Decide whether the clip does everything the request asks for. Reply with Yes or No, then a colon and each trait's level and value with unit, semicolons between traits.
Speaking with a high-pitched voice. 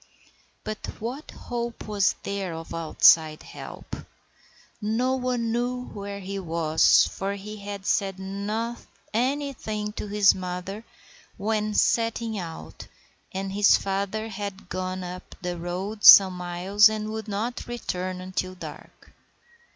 Yes: high, 200 Hz